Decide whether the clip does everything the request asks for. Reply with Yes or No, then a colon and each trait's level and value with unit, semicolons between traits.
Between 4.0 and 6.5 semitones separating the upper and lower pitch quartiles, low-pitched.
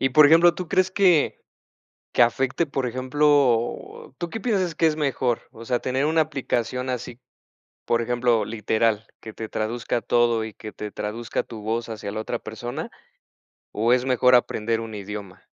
Yes: average, 4.3 semitones; low, 120 Hz